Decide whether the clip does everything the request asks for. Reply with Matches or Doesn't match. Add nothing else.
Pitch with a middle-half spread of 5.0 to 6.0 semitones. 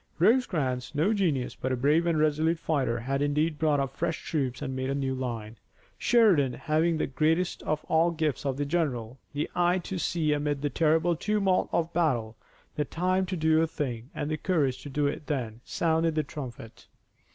Doesn't match